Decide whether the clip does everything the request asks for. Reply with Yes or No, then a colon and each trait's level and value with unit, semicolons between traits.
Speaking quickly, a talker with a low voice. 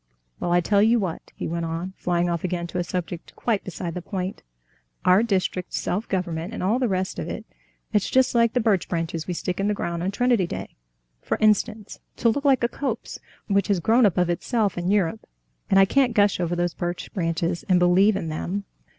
No: fast, 215 wpm; medium, 185 Hz